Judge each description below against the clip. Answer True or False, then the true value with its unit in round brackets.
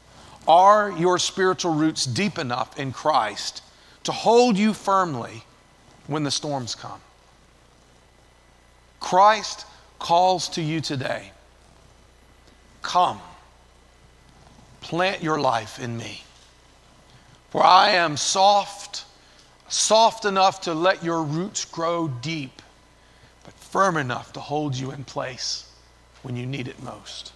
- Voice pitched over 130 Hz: True (140 Hz)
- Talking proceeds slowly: True (115 wpm)